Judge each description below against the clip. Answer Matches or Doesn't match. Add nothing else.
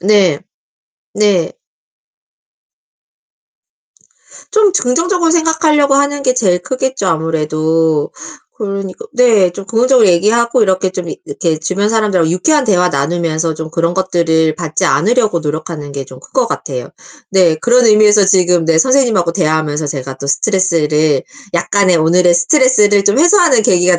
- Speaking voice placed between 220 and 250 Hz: Doesn't match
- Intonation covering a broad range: Matches